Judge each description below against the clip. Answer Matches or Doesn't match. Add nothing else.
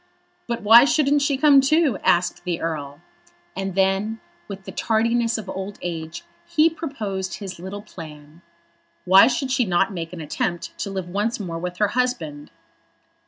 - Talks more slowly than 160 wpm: Doesn't match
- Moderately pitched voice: Doesn't match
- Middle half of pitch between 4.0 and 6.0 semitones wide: Matches